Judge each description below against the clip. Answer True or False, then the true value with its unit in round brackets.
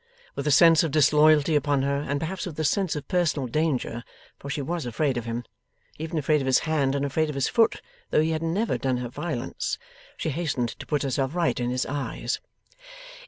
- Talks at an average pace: False (210 wpm)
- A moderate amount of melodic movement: True (3.2 semitones)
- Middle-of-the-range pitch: True (150 Hz)